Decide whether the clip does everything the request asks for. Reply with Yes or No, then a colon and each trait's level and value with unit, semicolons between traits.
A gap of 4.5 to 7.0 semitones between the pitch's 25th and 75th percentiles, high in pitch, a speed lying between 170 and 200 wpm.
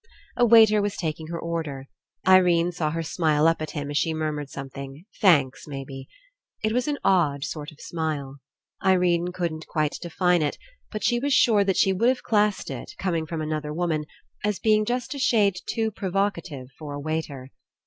No: average, 4.8 semitones; medium, 165 Hz; average, 195 wpm